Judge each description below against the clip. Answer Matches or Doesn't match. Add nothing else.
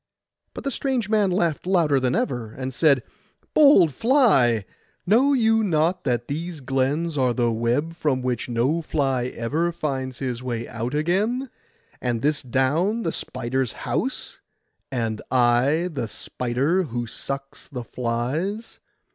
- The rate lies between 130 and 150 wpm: Matches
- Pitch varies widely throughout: Matches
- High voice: Doesn't match